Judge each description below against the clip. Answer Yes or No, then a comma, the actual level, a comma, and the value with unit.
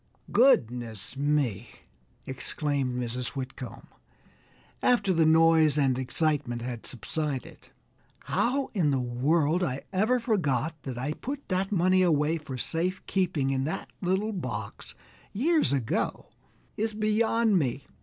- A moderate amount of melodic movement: No, wide, 6.4 semitones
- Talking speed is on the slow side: Yes, slow, 125 wpm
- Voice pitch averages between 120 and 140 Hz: No, medium, 155 Hz